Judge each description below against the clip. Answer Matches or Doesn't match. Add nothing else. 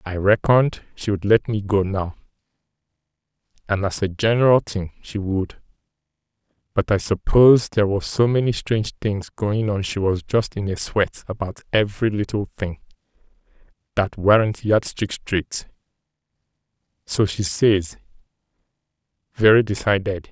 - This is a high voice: Doesn't match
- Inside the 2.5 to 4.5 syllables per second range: Matches